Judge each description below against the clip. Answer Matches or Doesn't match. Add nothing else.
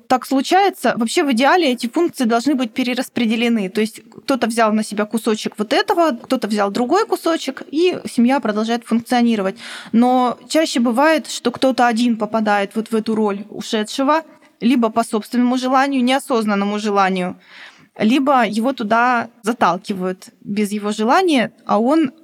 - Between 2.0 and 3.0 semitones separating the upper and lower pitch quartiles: Doesn't match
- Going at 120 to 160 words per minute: Matches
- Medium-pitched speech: Doesn't match